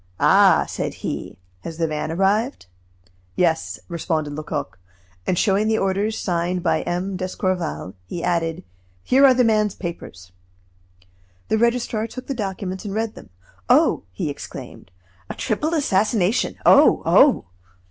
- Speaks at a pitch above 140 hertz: Yes, high, 190 Hz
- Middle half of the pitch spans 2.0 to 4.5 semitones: No, average, 4.9 semitones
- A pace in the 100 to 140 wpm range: Yes, slow, 135 wpm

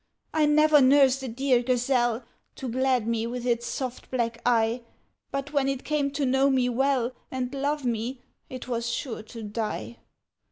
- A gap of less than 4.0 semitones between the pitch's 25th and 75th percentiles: Yes, narrow, 2.6 semitones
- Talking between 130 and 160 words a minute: No, average, 170 wpm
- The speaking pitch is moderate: No, very high, 255 Hz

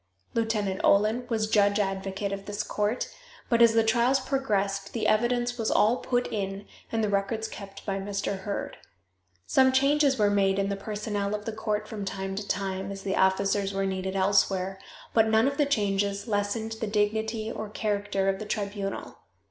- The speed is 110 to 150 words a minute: No, average, 180 wpm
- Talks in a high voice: Yes, high, 205 Hz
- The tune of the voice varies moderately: No, narrow, 2.2 semitones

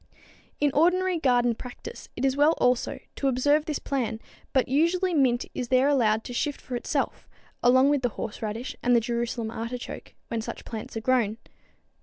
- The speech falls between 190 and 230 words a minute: No, average, 175 wpm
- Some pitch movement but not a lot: Yes, average, 3.5 semitones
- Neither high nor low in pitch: No, very high, 255 Hz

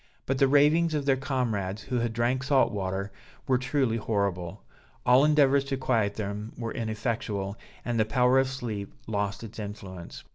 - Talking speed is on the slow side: No, average, 170 wpm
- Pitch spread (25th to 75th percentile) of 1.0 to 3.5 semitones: No, average, 4.6 semitones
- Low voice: Yes, low, 115 Hz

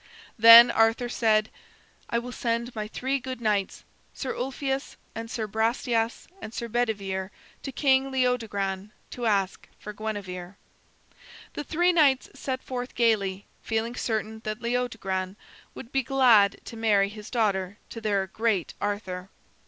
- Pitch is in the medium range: No, high, 225 Hz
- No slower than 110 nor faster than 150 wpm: Yes, average, 145 wpm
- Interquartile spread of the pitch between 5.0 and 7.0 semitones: No, average, 3.3 semitones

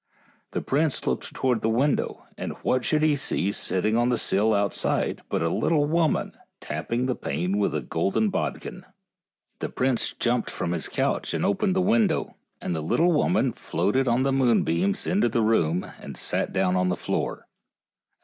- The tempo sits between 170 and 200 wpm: Yes, average, 180 wpm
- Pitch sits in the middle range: No, low, 115 Hz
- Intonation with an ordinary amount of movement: No, wide, 7.2 semitones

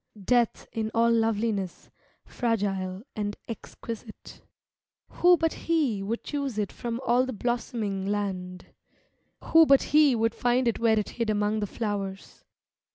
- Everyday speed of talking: Yes, average, 145 wpm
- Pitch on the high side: Yes, high, 225 Hz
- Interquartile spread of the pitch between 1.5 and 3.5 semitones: Yes, average, 3.0 semitones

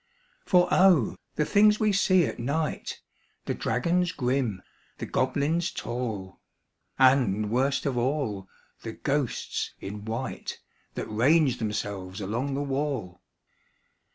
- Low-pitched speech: Yes, low, 130 Hz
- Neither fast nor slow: No, slow, 120 wpm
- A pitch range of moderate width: No, wide, 5.7 semitones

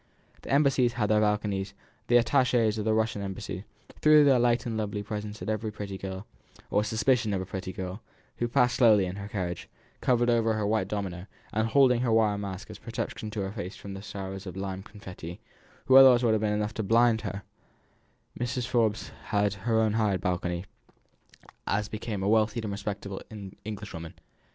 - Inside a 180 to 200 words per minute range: Yes, average, 195 wpm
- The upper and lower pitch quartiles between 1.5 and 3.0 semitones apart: Yes, narrow, 2.6 semitones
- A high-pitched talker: No, low, 105 Hz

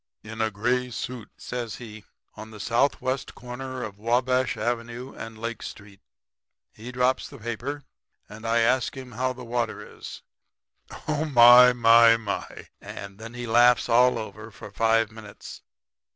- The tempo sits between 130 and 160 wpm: Yes, average, 150 wpm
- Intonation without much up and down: Yes, narrow, 2.2 semitones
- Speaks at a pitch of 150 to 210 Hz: No, low, 120 Hz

